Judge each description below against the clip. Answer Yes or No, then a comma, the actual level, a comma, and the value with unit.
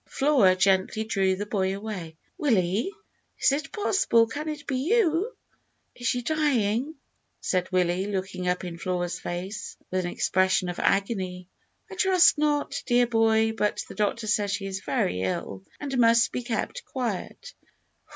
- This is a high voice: Yes, high, 210 Hz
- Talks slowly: No, average, 155 wpm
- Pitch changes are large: Yes, wide, 6.0 semitones